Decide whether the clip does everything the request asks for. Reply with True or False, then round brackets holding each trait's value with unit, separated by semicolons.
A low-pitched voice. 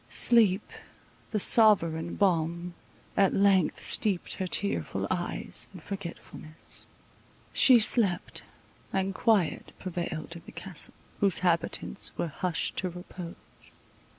False (185 Hz)